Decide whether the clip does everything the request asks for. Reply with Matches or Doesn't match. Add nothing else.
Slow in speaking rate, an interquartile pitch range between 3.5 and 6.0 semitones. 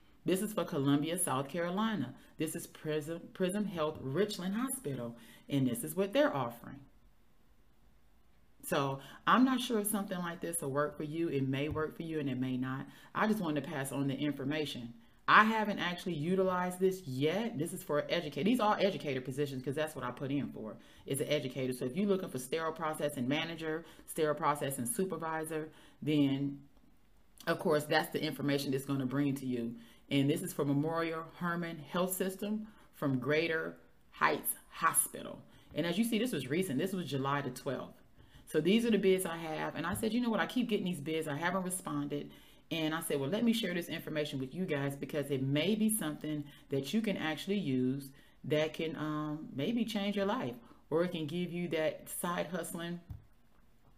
Doesn't match